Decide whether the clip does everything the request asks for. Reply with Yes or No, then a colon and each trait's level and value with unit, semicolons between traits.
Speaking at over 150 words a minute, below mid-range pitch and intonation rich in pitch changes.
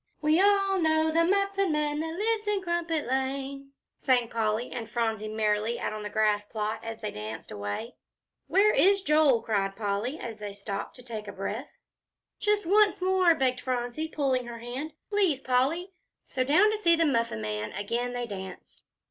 No: average, 175 wpm; very high, 255 Hz; wide, 7.4 semitones